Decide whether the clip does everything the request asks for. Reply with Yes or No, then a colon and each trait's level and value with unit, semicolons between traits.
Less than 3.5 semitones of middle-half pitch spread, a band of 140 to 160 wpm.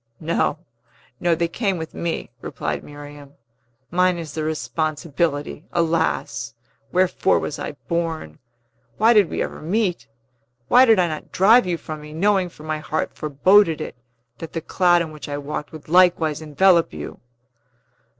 Yes: average, 3.1 semitones; average, 155 wpm